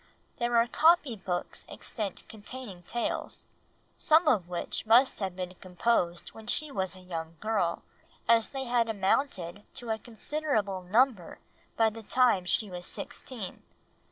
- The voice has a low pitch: No, high, 220 Hz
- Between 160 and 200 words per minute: No, average, 145 wpm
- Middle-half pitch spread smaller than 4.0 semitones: No, average, 4.7 semitones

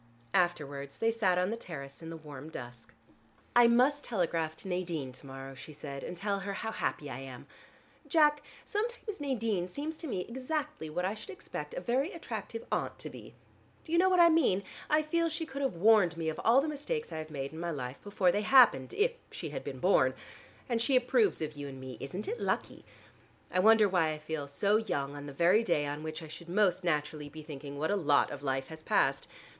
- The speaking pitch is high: No, medium, 180 Hz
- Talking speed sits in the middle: No, fast, 225 wpm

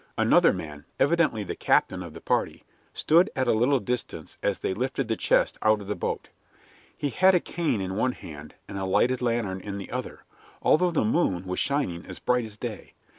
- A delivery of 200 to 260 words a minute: Yes, fast, 205 wpm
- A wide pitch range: Yes, wide, 5.8 semitones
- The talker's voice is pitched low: Yes, low, 110 Hz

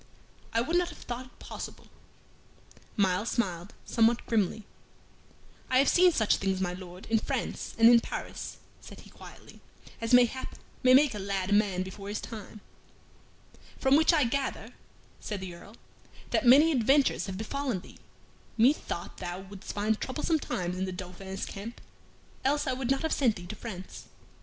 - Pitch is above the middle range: Yes, high, 220 Hz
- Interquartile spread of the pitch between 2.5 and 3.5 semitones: No, wide, 5.4 semitones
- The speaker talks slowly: No, average, 170 wpm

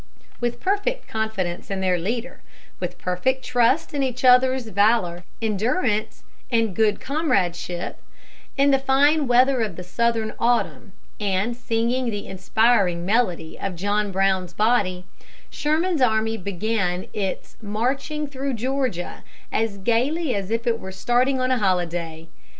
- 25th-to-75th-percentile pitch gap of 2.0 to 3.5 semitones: No, average, 5.2 semitones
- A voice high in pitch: Yes, high, 225 Hz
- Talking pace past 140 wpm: No, slow, 135 wpm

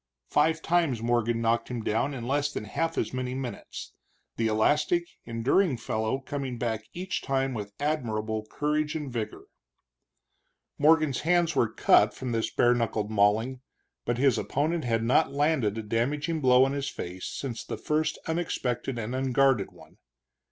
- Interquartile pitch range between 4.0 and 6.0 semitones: Yes, average, 4.5 semitones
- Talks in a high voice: No, low, 130 Hz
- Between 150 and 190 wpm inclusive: Yes, average, 160 wpm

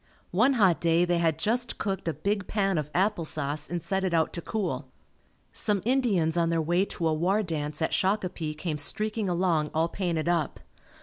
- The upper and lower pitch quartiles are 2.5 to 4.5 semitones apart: Yes, average, 3.7 semitones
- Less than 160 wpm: No, average, 195 wpm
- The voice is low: No, medium, 175 Hz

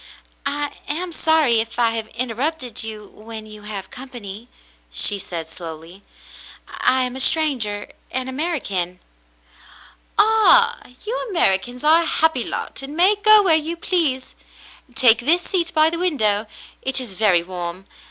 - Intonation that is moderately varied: No, wide, 7.3 semitones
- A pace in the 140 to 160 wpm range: Yes, average, 150 wpm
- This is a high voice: Yes, very high, 255 Hz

